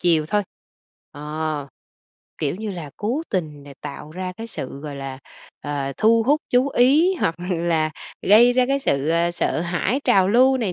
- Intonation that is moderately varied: No, wide, 7.8 semitones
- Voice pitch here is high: No, medium, 175 Hz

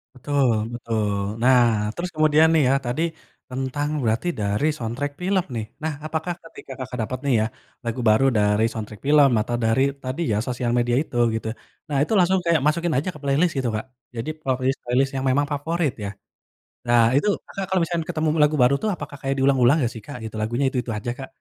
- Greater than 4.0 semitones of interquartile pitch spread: Yes, average, 4.4 semitones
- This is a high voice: No, low, 135 Hz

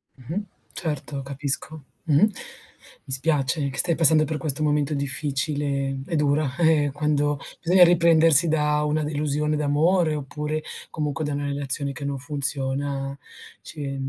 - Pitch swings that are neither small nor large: No, narrow, 1.9 semitones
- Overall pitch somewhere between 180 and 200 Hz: No, medium, 150 Hz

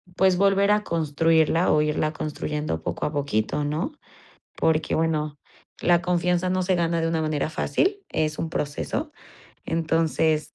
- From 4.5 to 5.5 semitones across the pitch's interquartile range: No, average, 2.7 semitones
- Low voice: No, medium, 160 Hz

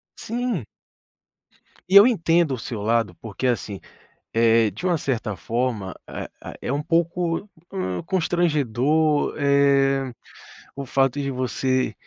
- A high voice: No, low, 135 Hz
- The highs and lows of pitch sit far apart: Yes, wide, 6.0 semitones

